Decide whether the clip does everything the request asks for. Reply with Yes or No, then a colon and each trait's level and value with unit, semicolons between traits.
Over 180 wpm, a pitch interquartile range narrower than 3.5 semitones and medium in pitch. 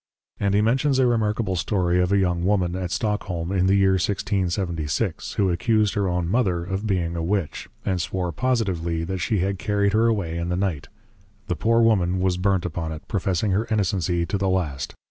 No: fast, 205 wpm; average, 2.9 semitones; very low, 95 Hz